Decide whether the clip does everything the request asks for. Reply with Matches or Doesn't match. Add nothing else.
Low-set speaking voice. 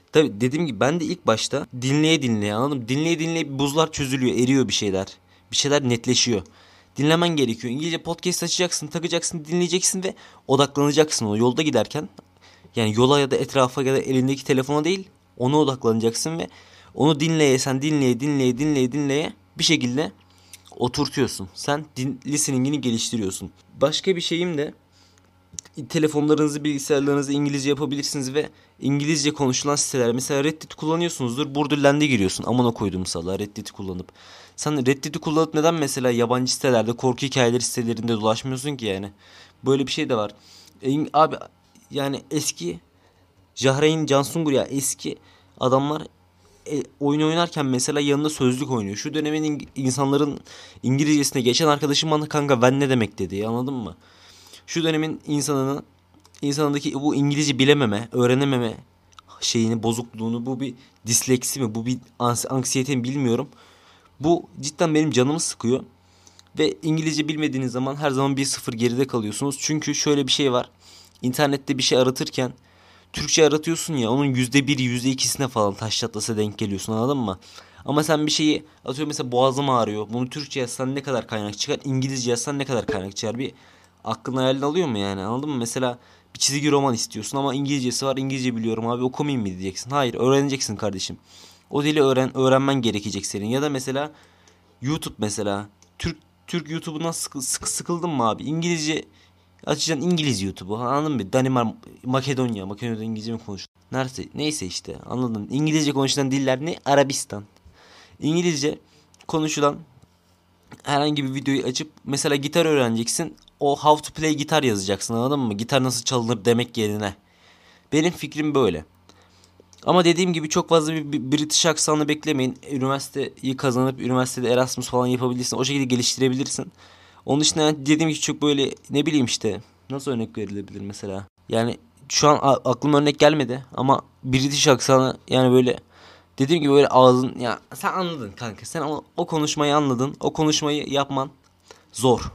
Matches